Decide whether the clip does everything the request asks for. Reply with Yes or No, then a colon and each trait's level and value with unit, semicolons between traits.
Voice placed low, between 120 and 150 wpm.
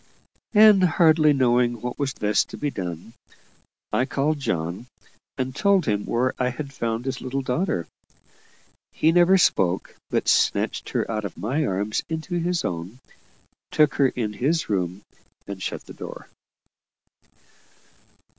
Yes: low, 130 Hz; average, 145 wpm